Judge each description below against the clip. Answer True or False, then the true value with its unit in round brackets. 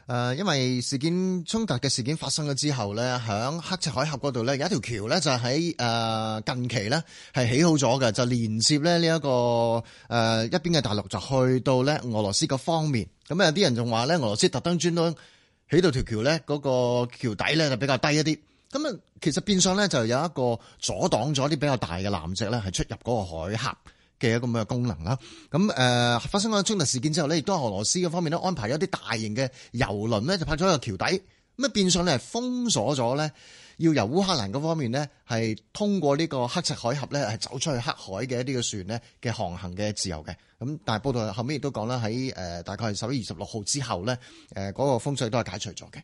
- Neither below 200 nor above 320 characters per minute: False (335 characters per minute)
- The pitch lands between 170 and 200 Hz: False (130 Hz)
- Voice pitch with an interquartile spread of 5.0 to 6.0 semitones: True (5.5 semitones)